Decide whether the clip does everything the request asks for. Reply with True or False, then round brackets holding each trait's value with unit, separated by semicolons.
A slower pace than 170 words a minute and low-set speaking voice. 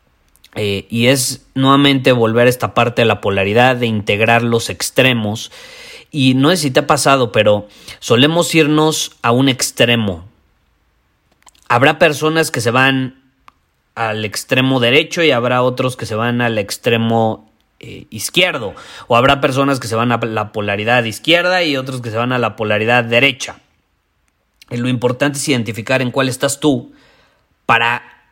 True (160 wpm; 120 Hz)